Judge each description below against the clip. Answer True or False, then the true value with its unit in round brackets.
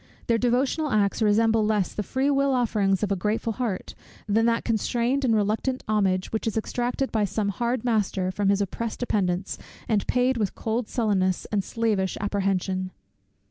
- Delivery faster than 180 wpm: False (170 wpm)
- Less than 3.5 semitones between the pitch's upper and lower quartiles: True (3.1 semitones)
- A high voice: True (215 Hz)